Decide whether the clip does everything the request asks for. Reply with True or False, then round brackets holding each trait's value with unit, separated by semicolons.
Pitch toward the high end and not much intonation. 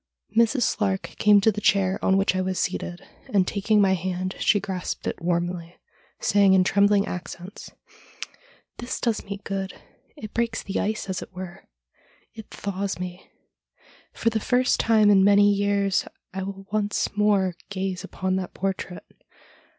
True (195 Hz; 1.8 semitones)